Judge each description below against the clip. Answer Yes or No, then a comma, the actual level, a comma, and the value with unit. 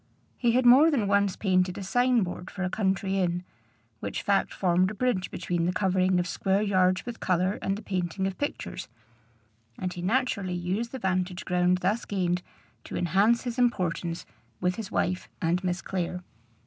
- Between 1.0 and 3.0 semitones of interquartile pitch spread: Yes, narrow, 2.5 semitones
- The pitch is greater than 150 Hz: Yes, high, 190 Hz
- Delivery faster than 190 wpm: No, average, 180 wpm